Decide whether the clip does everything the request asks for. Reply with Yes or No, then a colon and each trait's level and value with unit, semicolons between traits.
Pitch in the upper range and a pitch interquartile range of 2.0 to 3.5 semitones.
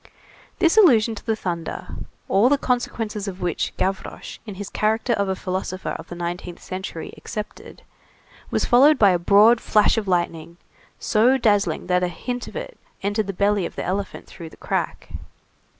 No: high, 200 Hz; average, 3.9 semitones